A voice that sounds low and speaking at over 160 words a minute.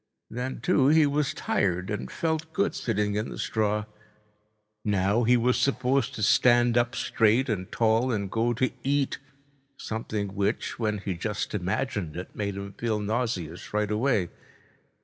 No: low, 110 Hz; average, 155 wpm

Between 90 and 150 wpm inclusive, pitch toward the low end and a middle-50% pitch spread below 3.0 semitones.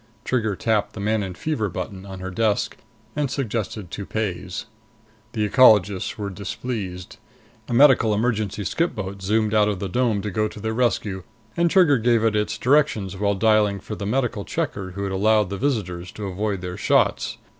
No: average, 175 wpm; low, 105 Hz; narrow, 2.6 semitones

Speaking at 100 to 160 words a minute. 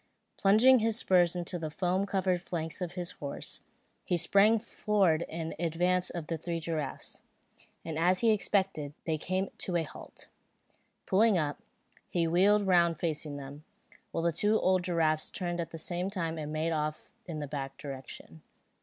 No: average, 170 wpm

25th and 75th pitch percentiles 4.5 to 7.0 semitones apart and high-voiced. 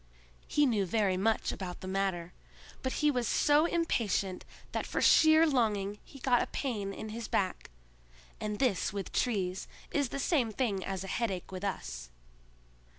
Yes: average, 5.2 semitones; high, 210 Hz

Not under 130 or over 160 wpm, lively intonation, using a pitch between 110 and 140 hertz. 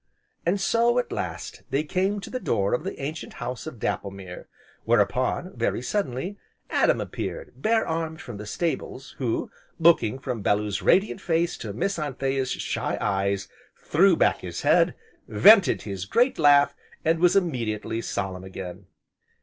Yes: average, 150 wpm; wide, 9.0 semitones; low, 135 Hz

